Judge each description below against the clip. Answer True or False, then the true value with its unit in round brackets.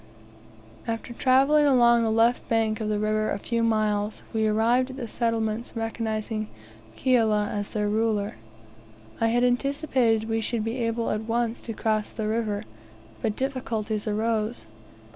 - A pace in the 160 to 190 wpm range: False (150 wpm)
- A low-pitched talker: False (225 Hz)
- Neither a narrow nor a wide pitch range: False (1.7 semitones)